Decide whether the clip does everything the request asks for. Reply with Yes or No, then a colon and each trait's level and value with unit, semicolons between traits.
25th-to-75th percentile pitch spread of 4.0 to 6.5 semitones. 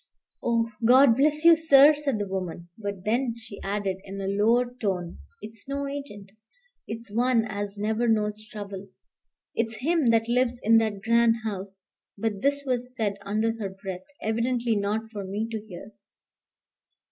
No: average, 3.2 semitones